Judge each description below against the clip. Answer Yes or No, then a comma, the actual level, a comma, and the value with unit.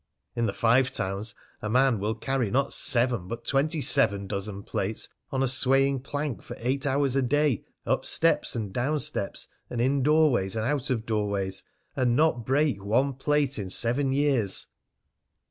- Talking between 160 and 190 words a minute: Yes, average, 170 wpm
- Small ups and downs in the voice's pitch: No, average, 4.3 semitones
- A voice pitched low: Yes, low, 125 Hz